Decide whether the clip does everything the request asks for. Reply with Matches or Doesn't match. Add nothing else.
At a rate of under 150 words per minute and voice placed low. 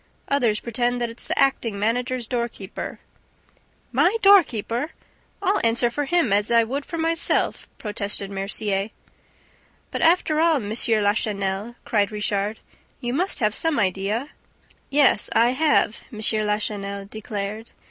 Doesn't match